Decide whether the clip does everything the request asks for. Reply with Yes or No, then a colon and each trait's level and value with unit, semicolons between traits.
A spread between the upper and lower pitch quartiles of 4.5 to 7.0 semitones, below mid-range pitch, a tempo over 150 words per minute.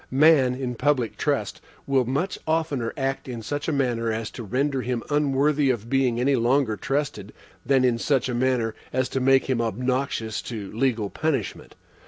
No: average, 2.9 semitones; low, 130 Hz; average, 175 wpm